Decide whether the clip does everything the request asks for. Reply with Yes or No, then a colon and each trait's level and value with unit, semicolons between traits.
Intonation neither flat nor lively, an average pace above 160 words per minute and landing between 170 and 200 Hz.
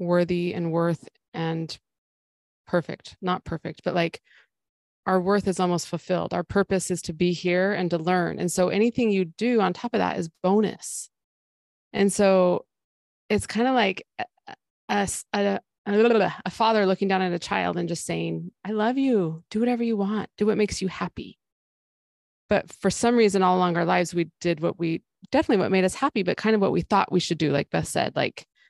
Yes: average, 3.4 semitones; average, 200 wpm; medium, 185 Hz